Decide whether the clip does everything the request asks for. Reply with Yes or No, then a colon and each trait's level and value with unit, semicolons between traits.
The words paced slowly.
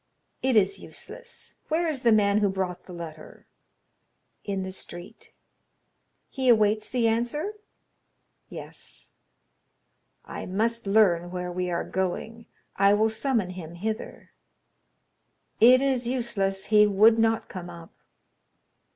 Yes: slow, 125 wpm